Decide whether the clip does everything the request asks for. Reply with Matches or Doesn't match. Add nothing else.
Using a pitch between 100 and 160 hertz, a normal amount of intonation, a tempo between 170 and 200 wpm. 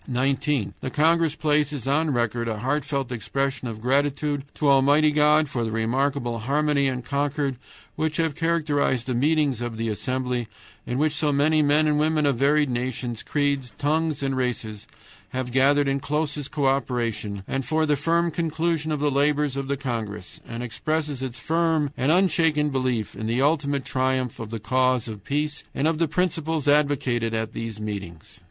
Matches